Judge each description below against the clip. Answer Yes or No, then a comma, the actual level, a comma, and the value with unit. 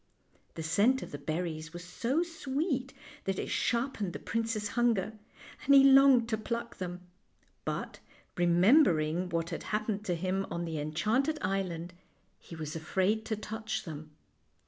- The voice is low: No, high, 195 Hz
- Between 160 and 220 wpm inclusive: No, average, 150 wpm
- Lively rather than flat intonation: Yes, wide, 5.8 semitones